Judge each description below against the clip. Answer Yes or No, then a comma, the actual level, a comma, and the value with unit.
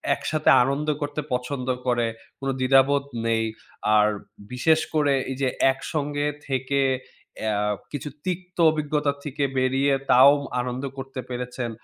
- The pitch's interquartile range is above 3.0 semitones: No, narrow, 2.4 semitones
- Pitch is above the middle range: No, medium, 140 Hz